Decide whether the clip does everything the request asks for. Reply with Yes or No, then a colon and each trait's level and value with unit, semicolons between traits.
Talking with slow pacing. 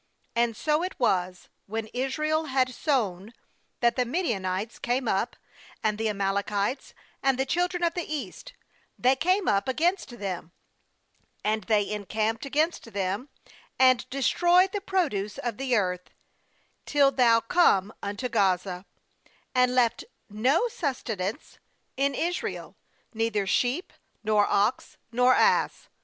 Yes: slow, 130 wpm